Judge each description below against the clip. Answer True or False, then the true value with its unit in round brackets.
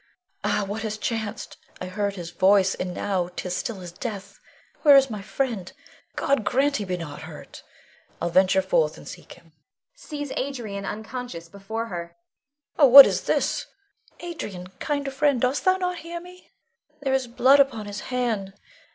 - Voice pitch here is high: True (215 Hz)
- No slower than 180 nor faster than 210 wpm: False (170 wpm)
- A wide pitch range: True (6.1 semitones)